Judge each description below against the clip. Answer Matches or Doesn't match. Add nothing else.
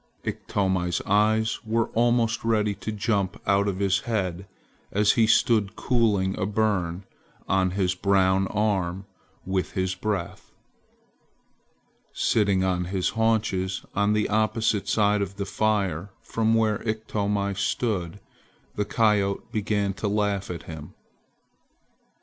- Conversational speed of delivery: Doesn't match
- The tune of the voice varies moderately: Doesn't match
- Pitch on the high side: Doesn't match